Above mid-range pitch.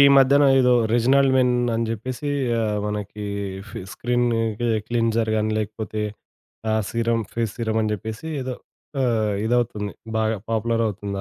No: low, 115 Hz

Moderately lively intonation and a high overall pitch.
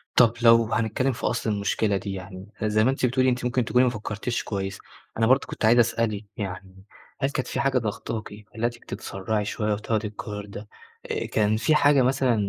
No: average, 3.1 semitones; low, 110 Hz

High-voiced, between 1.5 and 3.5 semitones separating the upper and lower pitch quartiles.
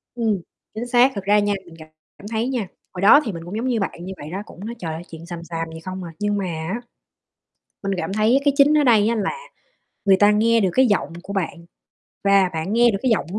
No: high, 200 Hz; average, 4.5 semitones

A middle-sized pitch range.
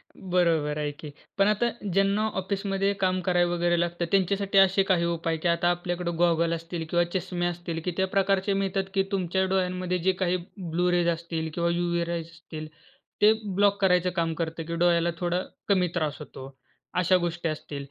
No: narrow, 2.1 semitones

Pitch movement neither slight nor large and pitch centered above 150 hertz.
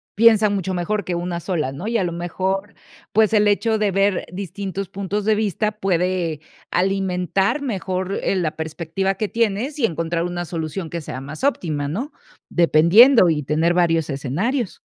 Yes: average, 3.6 semitones; medium, 185 Hz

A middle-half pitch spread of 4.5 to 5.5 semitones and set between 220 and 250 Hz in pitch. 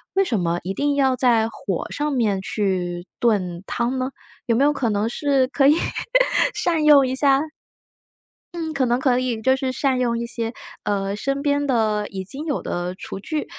Yes: average, 5.1 semitones; high, 245 Hz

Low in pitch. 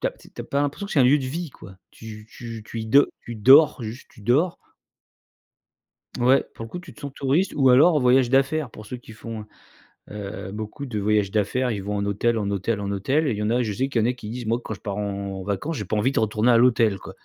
Yes: low, 115 Hz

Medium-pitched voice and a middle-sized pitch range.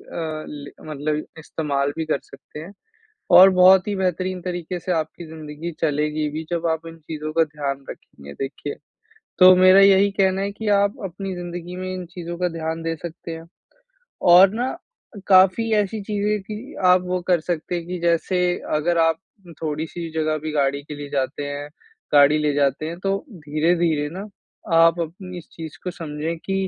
Yes: medium, 165 Hz; average, 3.3 semitones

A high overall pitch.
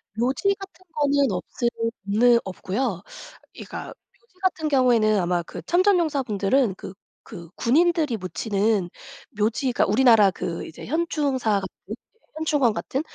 Yes: high, 245 Hz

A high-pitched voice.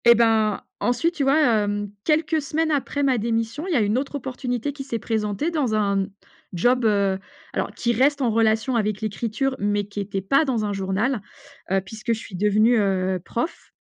Yes: high, 225 Hz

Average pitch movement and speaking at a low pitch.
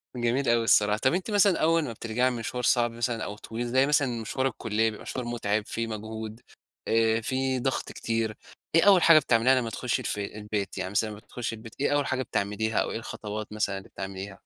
Yes: average, 3.2 semitones; low, 115 Hz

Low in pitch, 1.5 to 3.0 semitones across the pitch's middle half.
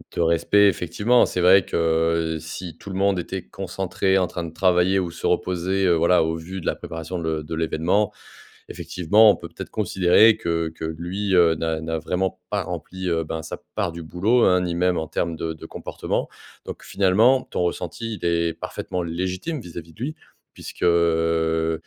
Yes: very low, 85 Hz; narrow, 2.6 semitones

